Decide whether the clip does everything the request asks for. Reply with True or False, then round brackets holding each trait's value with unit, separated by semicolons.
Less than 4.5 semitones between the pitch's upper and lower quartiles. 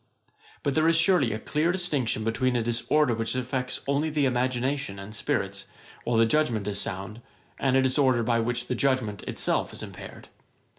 True (3.7 semitones)